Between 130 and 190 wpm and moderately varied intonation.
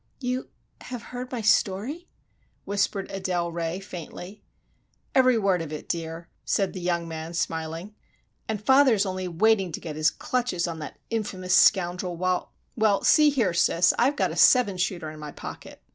Yes: average, 165 wpm; average, 4.6 semitones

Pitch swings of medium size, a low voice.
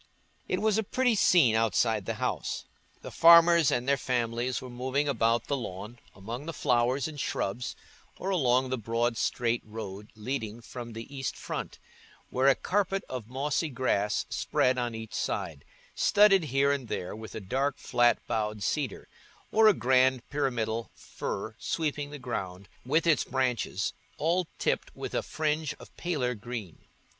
Yes: average, 4.3 semitones; low, 125 Hz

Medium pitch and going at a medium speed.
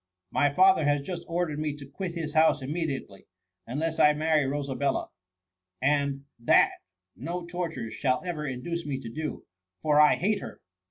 Yes: medium, 150 Hz; average, 165 wpm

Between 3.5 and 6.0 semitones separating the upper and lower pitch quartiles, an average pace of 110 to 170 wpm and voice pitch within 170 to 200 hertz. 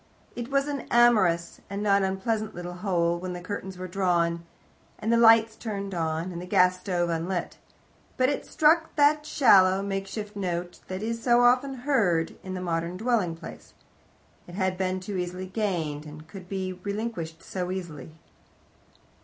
Yes: average, 4.0 semitones; average, 165 wpm; high, 190 Hz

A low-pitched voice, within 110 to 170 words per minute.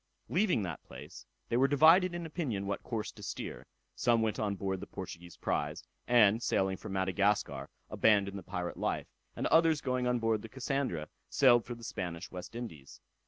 No: low, 110 Hz; average, 180 wpm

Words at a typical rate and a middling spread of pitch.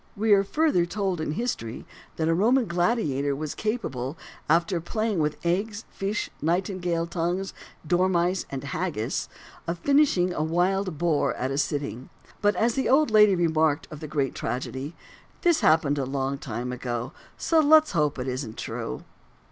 No: average, 160 wpm; wide, 5.8 semitones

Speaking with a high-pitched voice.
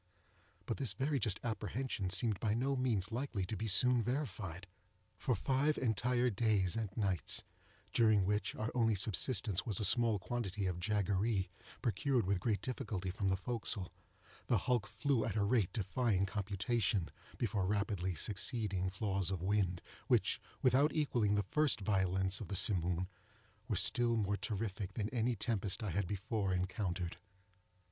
No: low, 105 Hz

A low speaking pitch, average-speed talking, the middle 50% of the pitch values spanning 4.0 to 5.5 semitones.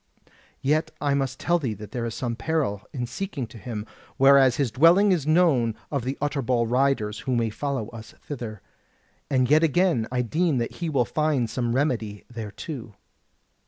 Yes: low, 130 Hz; average, 175 wpm; average, 4.3 semitones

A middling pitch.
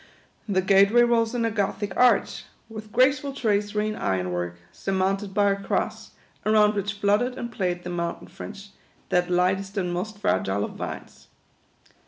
No: high, 200 Hz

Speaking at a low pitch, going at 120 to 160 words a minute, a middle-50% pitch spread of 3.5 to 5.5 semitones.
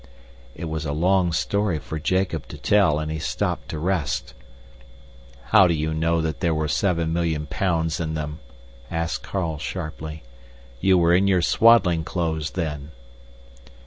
No: very low, 80 Hz; average, 150 wpm; narrow, 2.5 semitones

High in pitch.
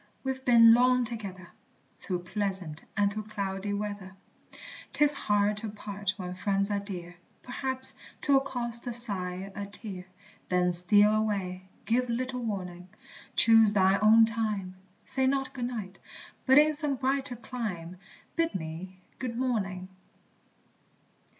Yes: high, 210 Hz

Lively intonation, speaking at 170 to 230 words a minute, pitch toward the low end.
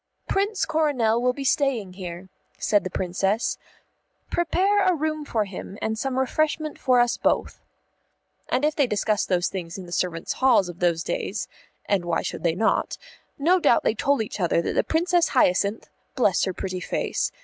No: wide, 8.2 semitones; average, 180 wpm; high, 225 Hz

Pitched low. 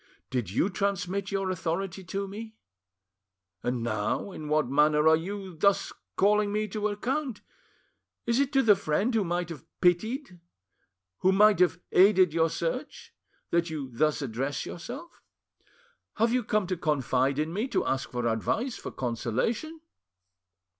No: medium, 185 Hz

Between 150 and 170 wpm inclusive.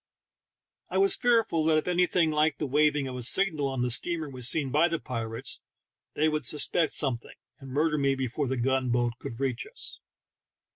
No: average, 190 wpm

